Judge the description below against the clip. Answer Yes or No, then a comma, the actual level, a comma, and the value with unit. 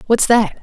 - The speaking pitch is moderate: No, high, 220 Hz